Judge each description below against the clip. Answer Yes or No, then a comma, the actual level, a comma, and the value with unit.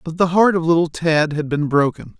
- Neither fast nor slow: No, fast, 245 wpm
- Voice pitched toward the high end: No, medium, 165 Hz